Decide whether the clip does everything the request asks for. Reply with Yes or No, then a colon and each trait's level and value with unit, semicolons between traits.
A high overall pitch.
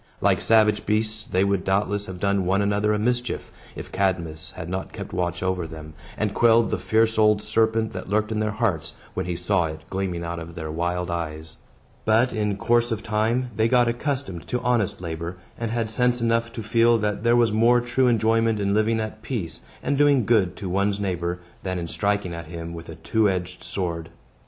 No: low, 105 Hz